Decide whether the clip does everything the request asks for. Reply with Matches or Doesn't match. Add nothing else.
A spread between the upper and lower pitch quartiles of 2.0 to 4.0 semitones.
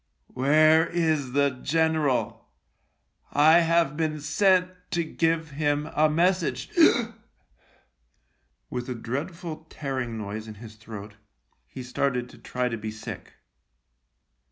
Doesn't match